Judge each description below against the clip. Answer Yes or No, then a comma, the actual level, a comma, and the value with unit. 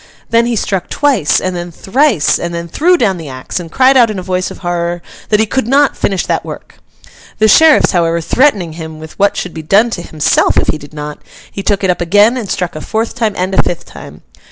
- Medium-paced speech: No, fast, 240 wpm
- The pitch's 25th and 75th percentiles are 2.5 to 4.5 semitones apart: No, average, 5.2 semitones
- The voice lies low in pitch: No, high, 190 Hz